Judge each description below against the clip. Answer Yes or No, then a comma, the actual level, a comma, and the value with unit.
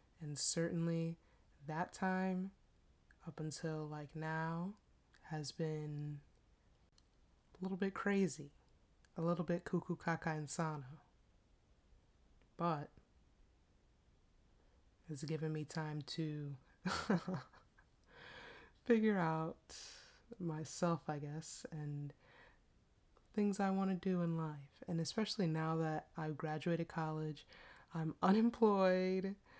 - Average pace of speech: No, slow, 95 wpm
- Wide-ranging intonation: No, average, 3.3 semitones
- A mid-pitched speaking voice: Yes, medium, 160 Hz